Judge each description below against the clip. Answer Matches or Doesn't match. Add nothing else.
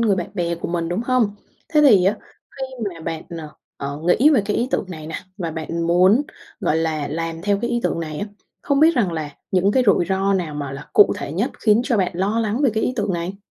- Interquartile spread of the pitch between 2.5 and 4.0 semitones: Doesn't match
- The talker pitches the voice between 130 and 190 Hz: Matches